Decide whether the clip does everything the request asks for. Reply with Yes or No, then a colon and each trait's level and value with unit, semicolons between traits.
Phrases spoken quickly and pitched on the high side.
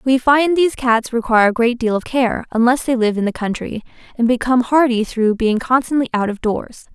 Yes: fast, 215 wpm; high, 240 Hz